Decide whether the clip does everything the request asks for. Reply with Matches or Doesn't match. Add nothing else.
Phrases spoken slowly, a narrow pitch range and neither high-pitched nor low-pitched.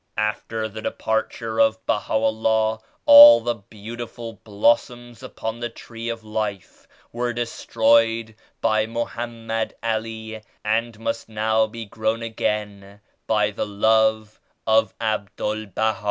Doesn't match